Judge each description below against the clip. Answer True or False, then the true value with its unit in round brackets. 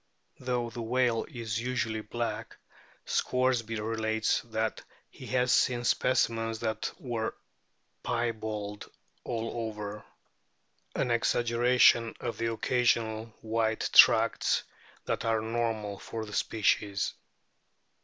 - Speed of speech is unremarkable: False (105 wpm)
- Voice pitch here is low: True (115 Hz)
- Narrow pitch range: True (1.4 semitones)